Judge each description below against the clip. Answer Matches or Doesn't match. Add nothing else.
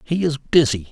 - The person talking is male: Matches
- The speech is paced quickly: Doesn't match